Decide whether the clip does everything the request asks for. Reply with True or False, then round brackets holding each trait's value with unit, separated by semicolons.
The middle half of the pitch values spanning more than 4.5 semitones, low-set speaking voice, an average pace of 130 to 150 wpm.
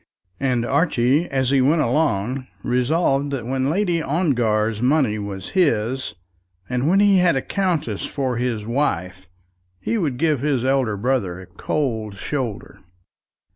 True (4.9 semitones; 130 Hz; 140 wpm)